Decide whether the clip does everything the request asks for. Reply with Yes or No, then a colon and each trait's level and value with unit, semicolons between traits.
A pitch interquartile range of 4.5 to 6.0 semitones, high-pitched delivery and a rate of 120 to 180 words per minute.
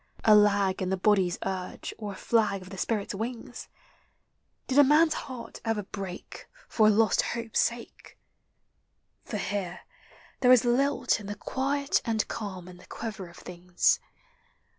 No: average, 3.6 semitones; high, 210 Hz; average, 160 wpm